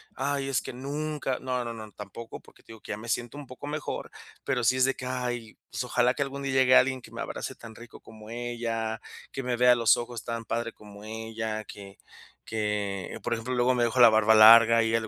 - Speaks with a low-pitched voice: Yes, low, 120 Hz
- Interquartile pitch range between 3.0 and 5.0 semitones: No, narrow, 2.4 semitones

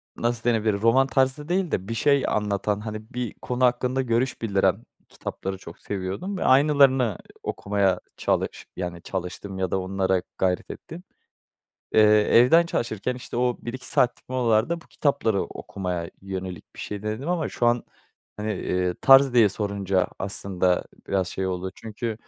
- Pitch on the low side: Yes, low, 110 Hz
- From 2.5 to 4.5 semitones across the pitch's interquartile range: No, average, 4.9 semitones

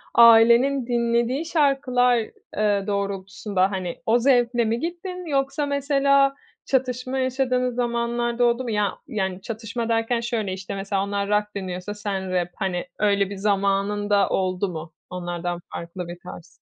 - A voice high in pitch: Yes, high, 225 Hz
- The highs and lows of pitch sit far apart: No, average, 4.3 semitones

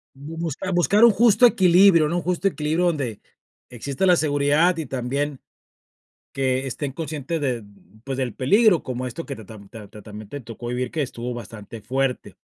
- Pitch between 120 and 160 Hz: Yes, medium, 140 Hz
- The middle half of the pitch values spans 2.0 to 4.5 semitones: No, wide, 5.4 semitones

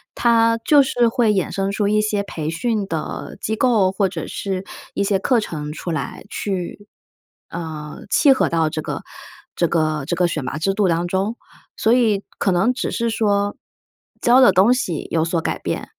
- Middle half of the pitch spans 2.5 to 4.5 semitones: No, average, 5.2 semitones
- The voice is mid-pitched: No, high, 195 Hz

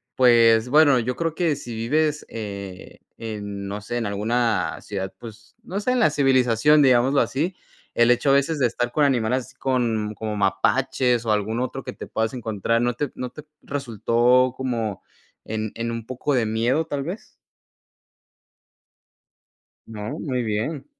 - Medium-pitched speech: No, low, 120 Hz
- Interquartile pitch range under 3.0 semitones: No, average, 3.7 semitones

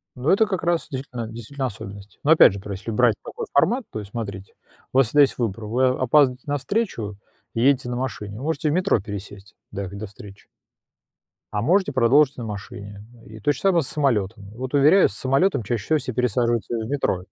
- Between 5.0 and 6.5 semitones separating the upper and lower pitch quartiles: Yes, average, 5.3 semitones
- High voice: No, low, 120 Hz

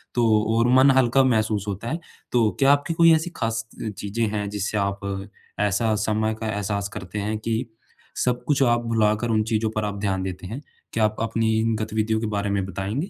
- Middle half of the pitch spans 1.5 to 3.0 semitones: Yes, narrow, 2.4 semitones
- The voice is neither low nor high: No, low, 110 Hz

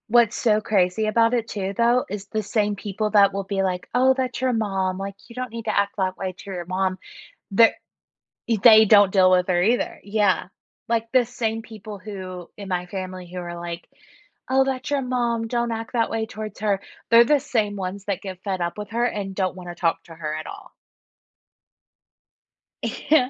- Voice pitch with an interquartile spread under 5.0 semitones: Yes, average, 3.6 semitones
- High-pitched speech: Yes, high, 205 Hz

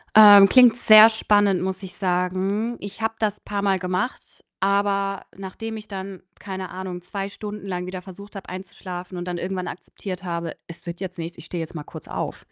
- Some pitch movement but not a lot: No, narrow, 2.1 semitones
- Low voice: No, high, 190 Hz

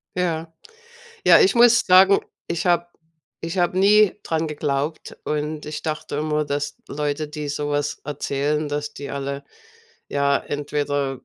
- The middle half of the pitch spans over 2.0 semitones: Yes, average, 2.7 semitones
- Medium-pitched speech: Yes, medium, 150 Hz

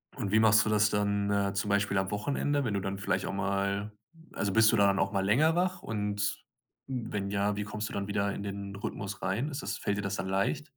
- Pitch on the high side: No, low, 100 Hz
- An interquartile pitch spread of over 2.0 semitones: No, narrow, 1.5 semitones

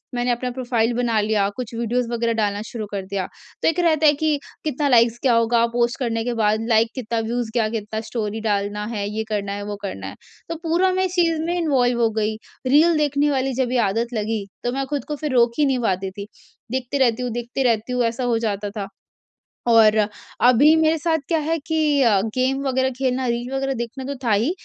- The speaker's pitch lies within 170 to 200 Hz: No, high, 240 Hz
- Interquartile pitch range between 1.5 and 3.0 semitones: No, average, 3.6 semitones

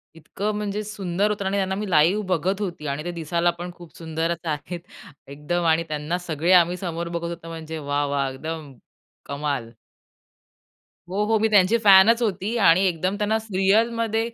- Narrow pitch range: No, average, 4.0 semitones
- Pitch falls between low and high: Yes, medium, 175 Hz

